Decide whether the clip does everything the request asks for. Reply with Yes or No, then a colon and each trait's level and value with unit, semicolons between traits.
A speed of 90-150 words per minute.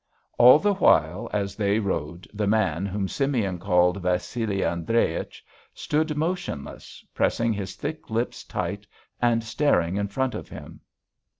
Yes: slow, 135 wpm